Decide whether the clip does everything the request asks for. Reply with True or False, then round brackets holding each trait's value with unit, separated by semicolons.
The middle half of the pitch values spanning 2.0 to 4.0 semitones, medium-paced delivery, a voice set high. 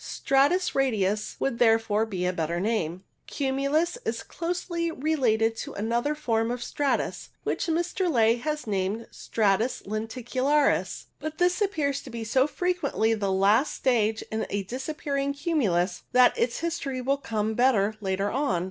False (5.3 semitones; 150 wpm; 245 Hz)